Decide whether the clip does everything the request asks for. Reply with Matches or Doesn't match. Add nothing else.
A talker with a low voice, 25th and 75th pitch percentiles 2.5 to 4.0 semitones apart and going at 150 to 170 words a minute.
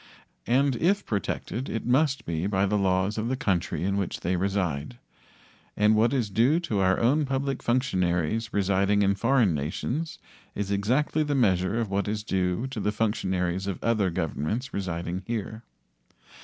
Doesn't match